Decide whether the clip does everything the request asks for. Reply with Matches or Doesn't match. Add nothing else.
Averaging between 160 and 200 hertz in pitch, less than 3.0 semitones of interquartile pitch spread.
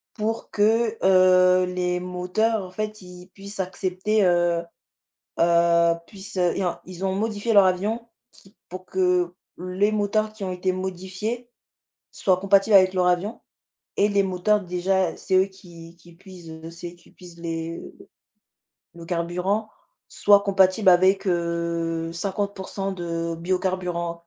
Matches